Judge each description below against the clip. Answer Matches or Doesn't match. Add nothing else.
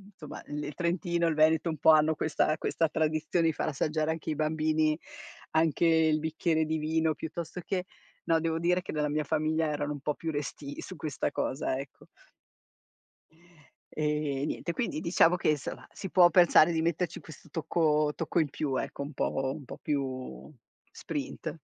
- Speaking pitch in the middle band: Matches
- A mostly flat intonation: Matches